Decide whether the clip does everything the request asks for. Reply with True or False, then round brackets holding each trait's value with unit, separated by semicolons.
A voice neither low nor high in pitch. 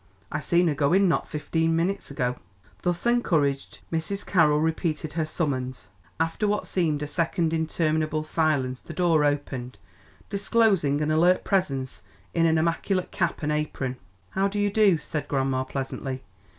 True (160 Hz)